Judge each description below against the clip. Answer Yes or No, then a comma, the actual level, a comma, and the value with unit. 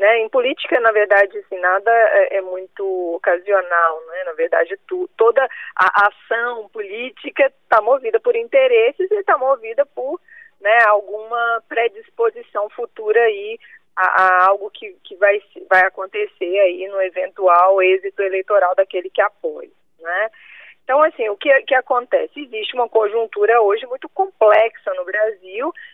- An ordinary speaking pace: Yes, average, 145 wpm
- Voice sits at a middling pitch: No, high, 235 Hz